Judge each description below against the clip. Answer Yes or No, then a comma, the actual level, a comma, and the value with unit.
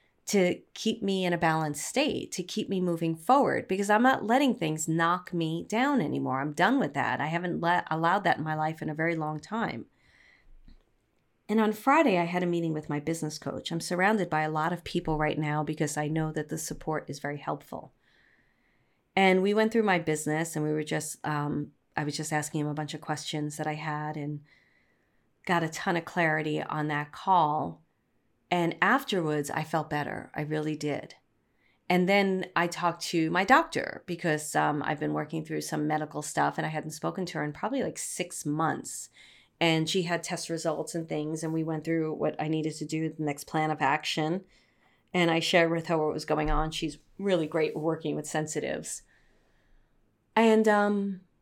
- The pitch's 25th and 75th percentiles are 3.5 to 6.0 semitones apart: No, average, 2.8 semitones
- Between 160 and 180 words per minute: No, average, 200 wpm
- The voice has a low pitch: No, medium, 160 Hz